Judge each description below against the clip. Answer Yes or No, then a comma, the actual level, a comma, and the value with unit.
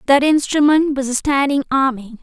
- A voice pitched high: Yes, very high, 275 Hz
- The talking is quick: No, average, 160 wpm